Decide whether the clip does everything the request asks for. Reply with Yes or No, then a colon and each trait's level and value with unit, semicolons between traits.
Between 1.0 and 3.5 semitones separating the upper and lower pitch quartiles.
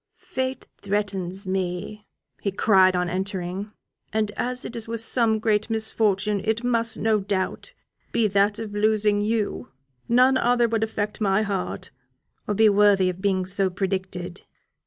Yes: narrow, 2.5 semitones